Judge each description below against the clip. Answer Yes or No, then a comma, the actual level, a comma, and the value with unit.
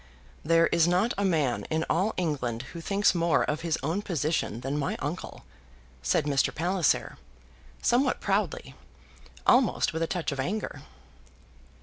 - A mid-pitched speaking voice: Yes, medium, 165 Hz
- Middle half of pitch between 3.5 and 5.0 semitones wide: Yes, average, 3.9 semitones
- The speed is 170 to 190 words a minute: No, average, 145 wpm